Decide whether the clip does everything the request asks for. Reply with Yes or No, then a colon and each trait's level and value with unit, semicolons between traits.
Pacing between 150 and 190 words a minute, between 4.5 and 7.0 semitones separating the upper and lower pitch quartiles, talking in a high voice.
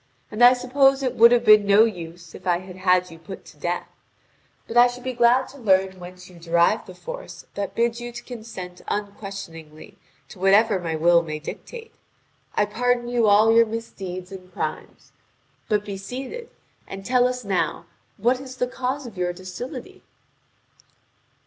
Yes: average, 175 wpm; average, 5.1 semitones; high, 205 Hz